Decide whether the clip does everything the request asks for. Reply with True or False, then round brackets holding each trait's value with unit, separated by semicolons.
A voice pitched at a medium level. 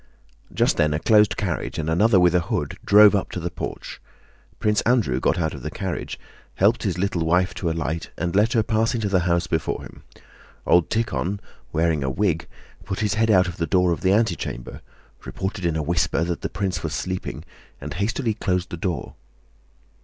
False (90 Hz)